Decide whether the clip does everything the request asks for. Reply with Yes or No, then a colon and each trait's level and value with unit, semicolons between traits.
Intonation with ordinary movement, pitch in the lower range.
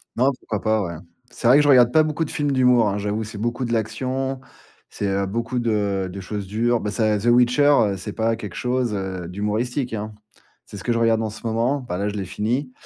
Yes: average, 3.2 semitones; low, 110 Hz